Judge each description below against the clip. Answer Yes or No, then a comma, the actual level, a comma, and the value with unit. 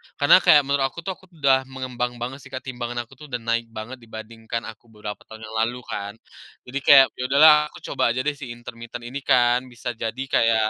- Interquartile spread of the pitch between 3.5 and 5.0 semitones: No, narrow, 2.6 semitones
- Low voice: Yes, low, 120 Hz